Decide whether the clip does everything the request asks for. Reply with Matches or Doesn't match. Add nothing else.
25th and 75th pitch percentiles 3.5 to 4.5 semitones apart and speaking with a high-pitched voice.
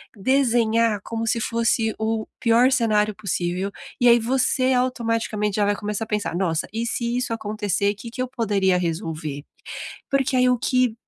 Doesn't match